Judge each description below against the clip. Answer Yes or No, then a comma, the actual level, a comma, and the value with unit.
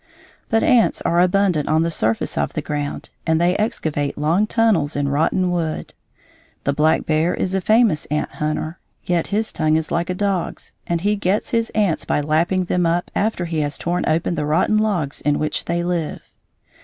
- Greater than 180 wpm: Yes, average, 190 wpm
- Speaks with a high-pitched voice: No, medium, 170 Hz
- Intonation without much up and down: No, average, 3.8 semitones